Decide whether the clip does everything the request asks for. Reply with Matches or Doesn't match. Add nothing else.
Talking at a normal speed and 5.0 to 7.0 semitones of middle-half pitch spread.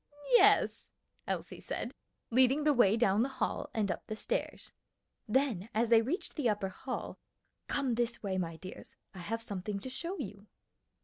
Doesn't match